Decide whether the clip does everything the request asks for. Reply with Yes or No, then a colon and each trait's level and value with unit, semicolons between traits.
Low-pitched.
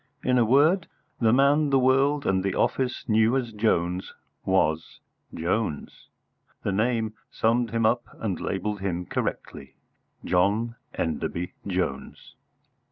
Yes: low, 110 Hz